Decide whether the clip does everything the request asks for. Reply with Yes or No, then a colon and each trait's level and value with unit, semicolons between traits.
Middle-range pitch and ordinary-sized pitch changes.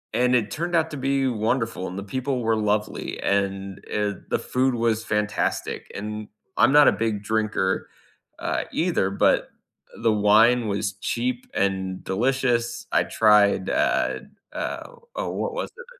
No: low, 110 Hz; average, 3.8 semitones